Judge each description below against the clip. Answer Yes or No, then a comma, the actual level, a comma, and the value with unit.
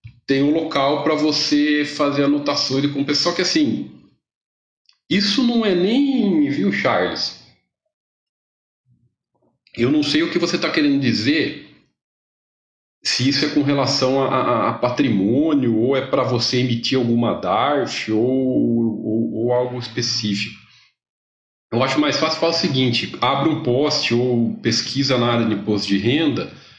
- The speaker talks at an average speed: Yes, average, 150 wpm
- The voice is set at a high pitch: No, low, 135 Hz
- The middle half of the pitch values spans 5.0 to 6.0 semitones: No, average, 4.6 semitones